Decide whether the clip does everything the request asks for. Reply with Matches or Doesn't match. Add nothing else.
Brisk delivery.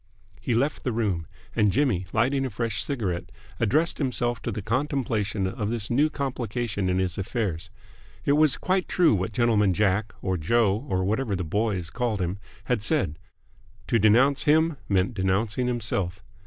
Doesn't match